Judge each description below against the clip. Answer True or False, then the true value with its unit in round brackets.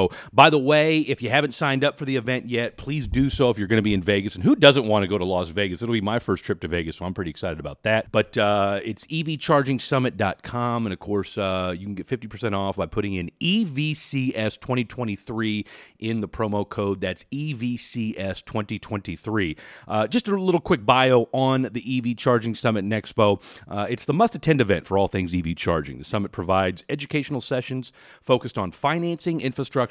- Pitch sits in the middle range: False (110 Hz)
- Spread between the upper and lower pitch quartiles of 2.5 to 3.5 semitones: False (5.1 semitones)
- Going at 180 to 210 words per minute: True (200 wpm)